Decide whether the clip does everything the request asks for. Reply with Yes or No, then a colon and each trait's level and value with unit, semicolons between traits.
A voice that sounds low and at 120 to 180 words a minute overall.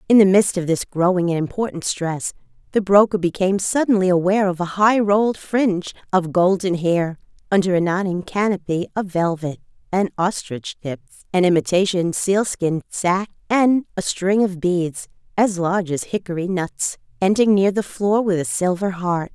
No: medium, 185 Hz; average, 165 wpm